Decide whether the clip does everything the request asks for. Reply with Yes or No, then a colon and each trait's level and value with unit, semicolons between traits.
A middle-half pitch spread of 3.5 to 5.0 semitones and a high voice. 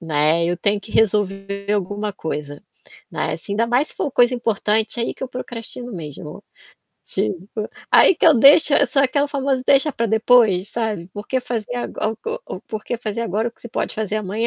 Yes: average, 3.8 semitones; high, 220 Hz